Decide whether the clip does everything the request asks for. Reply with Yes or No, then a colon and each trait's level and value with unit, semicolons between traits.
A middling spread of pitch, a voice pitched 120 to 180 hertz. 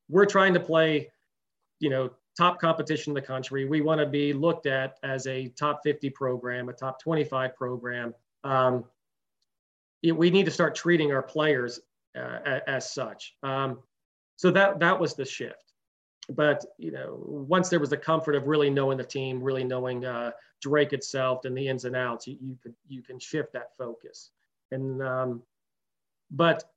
Yes: average, 3.3 semitones; low, 135 Hz